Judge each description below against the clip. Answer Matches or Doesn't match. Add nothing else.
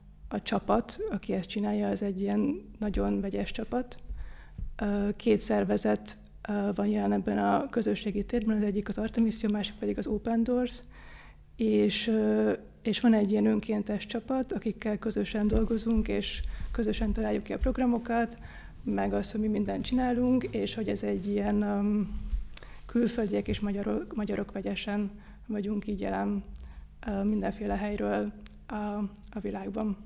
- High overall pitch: Matches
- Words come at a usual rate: Matches